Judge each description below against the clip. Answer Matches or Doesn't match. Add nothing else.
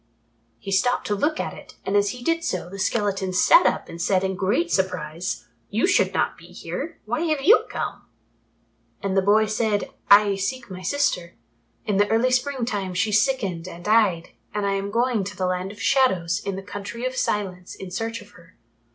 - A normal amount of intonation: Matches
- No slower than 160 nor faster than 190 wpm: Doesn't match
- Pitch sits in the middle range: Doesn't match